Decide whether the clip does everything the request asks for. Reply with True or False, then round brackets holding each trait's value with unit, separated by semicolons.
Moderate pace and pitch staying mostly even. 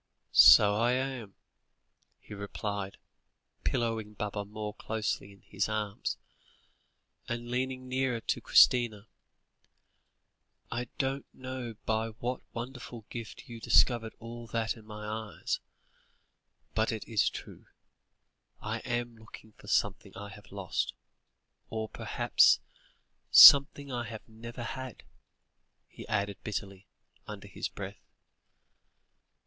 False (115 wpm; 2.3 semitones)